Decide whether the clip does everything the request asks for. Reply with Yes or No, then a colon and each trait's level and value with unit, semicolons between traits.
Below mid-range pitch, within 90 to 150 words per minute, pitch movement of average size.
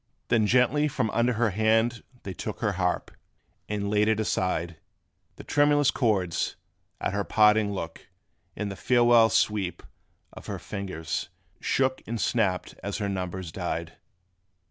Yes: low, 105 Hz; average, 145 wpm; average, 3.9 semitones